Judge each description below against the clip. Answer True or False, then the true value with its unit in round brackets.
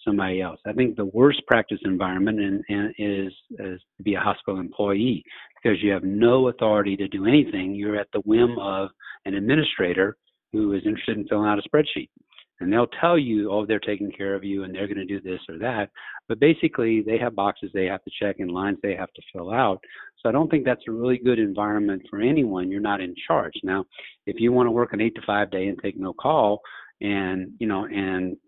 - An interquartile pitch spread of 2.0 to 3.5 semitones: True (2.6 semitones)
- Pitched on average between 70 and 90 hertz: False (105 Hz)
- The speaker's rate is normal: False (225 wpm)